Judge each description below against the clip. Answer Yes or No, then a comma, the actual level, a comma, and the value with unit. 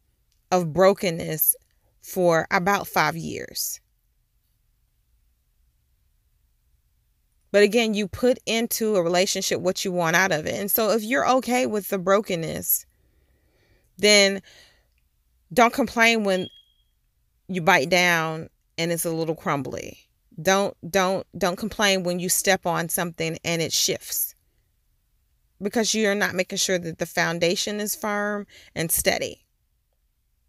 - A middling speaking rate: No, slow, 125 wpm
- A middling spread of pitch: Yes, average, 4.0 semitones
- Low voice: No, medium, 185 Hz